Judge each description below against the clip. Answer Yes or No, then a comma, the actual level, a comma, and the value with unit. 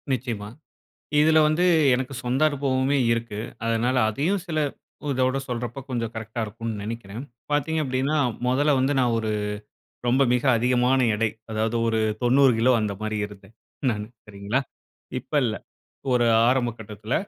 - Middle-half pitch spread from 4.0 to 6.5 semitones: No, average, 3.0 semitones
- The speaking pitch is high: No, low, 120 Hz